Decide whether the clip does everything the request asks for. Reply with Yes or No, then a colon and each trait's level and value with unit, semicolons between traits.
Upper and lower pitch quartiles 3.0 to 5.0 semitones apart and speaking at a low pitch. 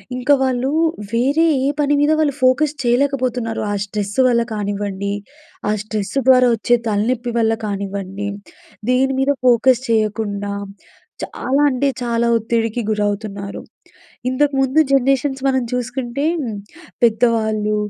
No: average, 3.7 semitones; high, 235 Hz